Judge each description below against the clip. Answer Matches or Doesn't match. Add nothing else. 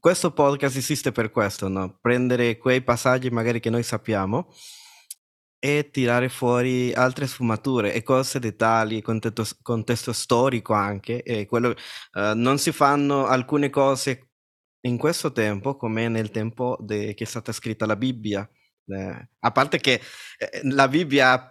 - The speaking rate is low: Doesn't match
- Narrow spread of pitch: Doesn't match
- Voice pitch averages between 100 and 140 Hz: Matches